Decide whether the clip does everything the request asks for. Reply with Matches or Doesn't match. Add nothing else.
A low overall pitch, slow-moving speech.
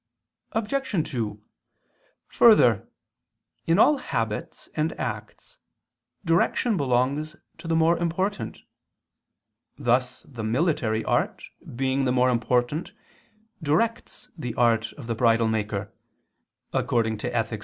Matches